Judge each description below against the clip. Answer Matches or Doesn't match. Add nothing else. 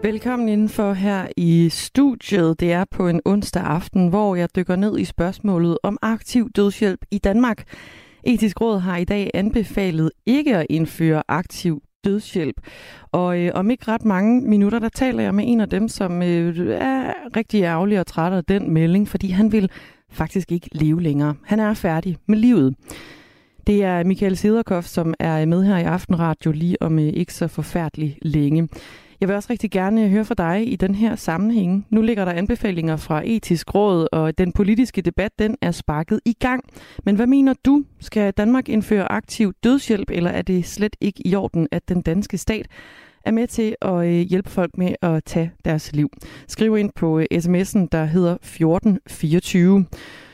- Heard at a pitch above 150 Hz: Matches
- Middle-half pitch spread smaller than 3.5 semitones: Doesn't match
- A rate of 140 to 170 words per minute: Doesn't match